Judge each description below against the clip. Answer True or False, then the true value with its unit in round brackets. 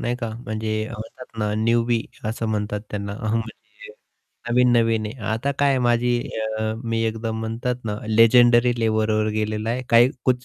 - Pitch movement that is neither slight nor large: False (1.7 semitones)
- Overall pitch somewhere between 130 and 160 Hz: False (115 Hz)